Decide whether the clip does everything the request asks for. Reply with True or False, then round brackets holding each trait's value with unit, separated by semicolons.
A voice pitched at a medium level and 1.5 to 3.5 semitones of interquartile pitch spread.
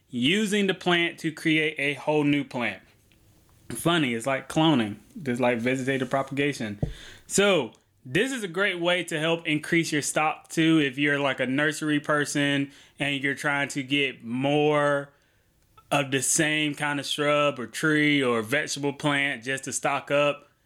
True (145 Hz; 2.4 semitones)